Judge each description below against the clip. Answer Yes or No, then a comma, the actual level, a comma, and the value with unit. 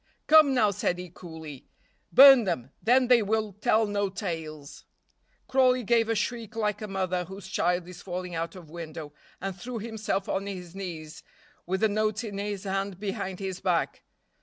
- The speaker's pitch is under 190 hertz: No, high, 195 Hz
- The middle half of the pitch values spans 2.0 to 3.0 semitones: No, average, 3.6 semitones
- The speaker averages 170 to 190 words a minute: Yes, average, 175 wpm